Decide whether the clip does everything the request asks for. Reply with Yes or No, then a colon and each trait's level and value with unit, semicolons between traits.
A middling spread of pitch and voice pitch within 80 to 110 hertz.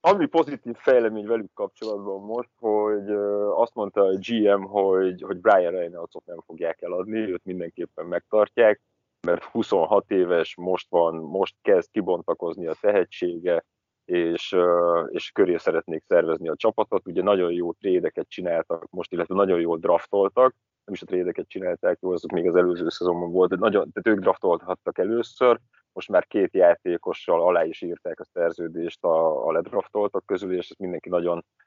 No: wide, 5.8 semitones; low, 105 Hz